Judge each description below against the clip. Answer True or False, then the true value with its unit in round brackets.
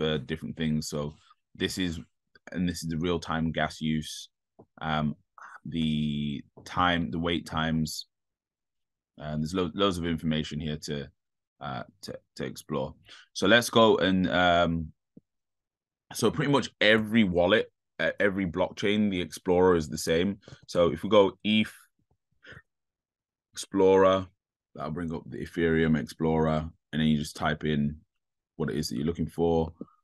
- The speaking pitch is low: True (80 Hz)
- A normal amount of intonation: True (3.4 semitones)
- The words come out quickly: False (145 wpm)